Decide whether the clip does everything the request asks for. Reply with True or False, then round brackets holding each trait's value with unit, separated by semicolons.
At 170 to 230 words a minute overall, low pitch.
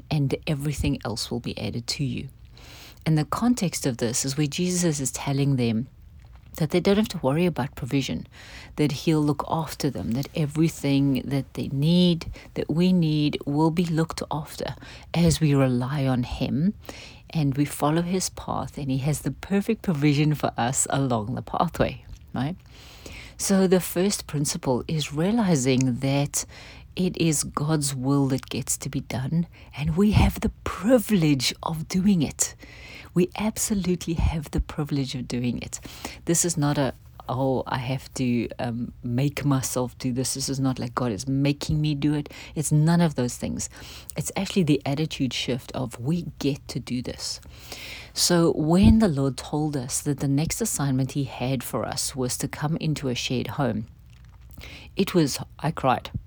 False (175 wpm; 145 Hz)